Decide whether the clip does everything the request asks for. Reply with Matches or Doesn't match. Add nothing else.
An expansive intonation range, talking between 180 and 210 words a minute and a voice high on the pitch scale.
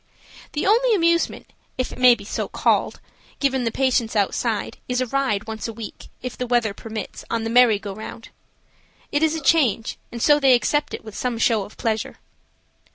Doesn't match